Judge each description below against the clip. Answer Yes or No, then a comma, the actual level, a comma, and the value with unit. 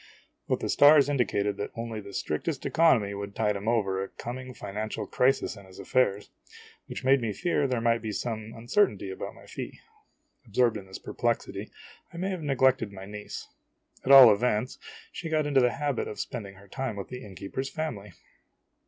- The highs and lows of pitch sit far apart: No, average, 4.9 semitones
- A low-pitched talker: Yes, low, 115 Hz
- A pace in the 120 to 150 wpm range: No, average, 190 wpm